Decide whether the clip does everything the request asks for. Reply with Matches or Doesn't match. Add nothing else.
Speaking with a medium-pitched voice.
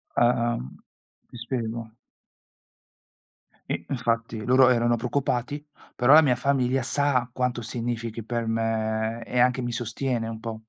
Doesn't match